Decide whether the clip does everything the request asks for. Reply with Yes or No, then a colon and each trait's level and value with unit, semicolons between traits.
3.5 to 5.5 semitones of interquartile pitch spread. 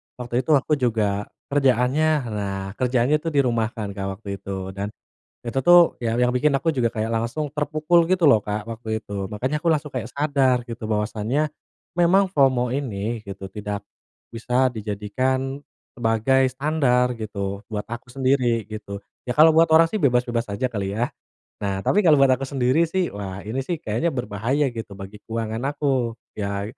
Yes: average, 4.7 semitones